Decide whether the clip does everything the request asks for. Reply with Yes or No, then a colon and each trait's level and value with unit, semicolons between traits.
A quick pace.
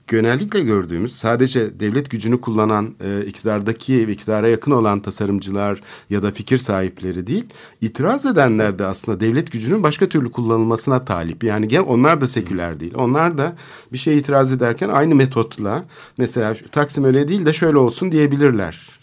Yes: fast, 160 wpm